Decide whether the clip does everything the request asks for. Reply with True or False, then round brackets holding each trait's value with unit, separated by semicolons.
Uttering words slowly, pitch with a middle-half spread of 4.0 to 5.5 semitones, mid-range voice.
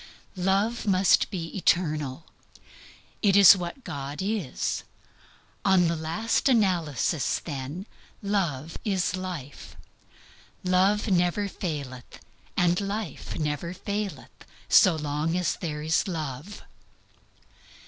True (100 wpm; 4.4 semitones; 175 Hz)